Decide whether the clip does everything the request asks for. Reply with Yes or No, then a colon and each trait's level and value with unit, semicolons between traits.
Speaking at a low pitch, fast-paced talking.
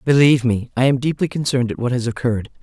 Yes: low, 130 Hz; fast, 230 wpm